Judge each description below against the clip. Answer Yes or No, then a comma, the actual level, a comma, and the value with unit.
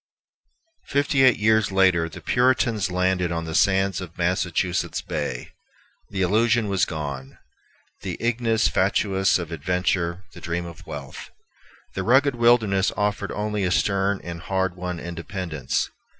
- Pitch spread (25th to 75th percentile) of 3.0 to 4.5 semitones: Yes, average, 3.6 semitones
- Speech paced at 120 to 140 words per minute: Yes, slow, 135 wpm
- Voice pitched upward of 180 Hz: No, very low, 95 Hz